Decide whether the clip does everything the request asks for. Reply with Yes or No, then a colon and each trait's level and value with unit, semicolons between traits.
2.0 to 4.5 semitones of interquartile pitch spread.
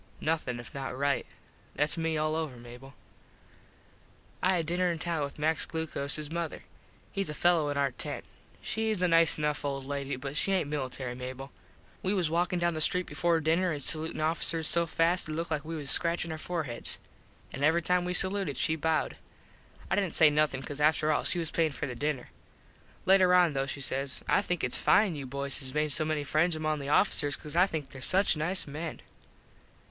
Yes: average, 3.2 semitones